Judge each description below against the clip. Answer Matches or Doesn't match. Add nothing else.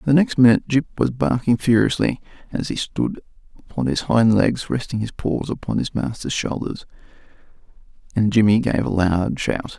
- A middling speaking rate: Matches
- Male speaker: Matches